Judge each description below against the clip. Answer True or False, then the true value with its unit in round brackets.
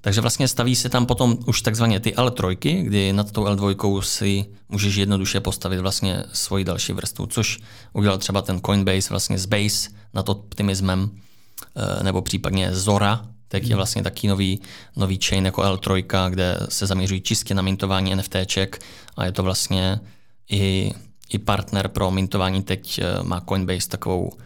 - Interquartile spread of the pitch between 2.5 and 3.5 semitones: False (2.0 semitones)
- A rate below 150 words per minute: False (155 wpm)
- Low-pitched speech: True (100 Hz)